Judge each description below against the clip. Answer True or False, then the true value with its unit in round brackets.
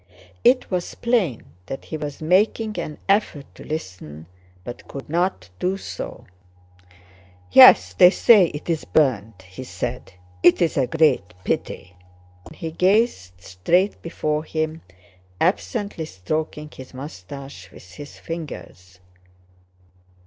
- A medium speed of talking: False (120 wpm)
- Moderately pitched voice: True (150 Hz)